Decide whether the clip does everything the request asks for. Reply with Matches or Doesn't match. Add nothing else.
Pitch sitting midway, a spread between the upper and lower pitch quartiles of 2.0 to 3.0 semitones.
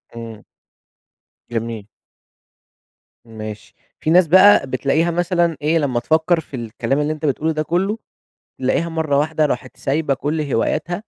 Doesn't match